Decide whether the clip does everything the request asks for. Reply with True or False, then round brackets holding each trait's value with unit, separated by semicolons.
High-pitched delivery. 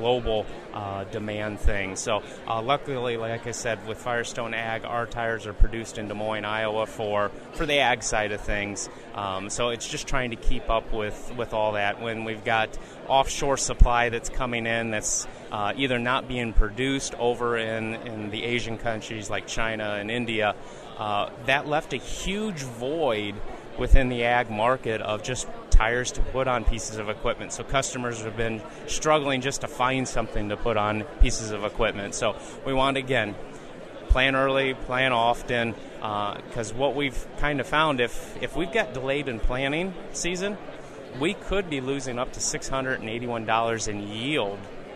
False (115 Hz)